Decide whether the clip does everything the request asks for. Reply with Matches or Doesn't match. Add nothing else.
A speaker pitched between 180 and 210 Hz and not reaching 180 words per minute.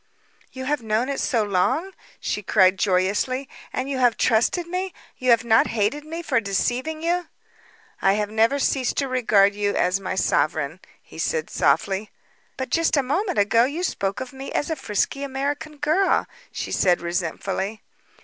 Doesn't match